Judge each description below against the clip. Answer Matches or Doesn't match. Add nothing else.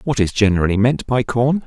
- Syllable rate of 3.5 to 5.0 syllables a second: Doesn't match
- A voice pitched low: Matches